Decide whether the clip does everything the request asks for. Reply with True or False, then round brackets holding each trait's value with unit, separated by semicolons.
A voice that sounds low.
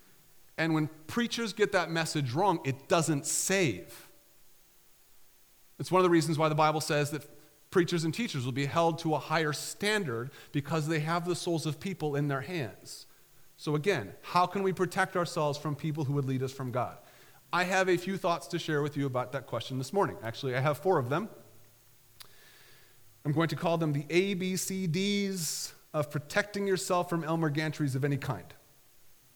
False (155 Hz)